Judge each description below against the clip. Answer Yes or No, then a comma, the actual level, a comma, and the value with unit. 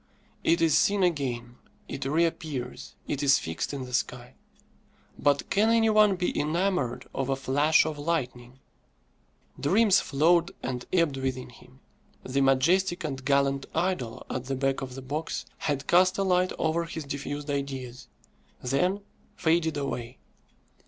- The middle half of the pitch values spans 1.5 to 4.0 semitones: No, average, 4.4 semitones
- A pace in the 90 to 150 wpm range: Yes, average, 145 wpm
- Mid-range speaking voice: Yes, medium, 145 Hz